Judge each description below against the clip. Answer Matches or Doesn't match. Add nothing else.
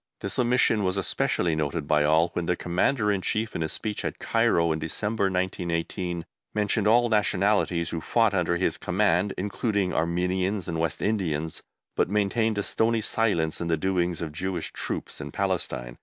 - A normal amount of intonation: Matches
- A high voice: Doesn't match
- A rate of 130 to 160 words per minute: Doesn't match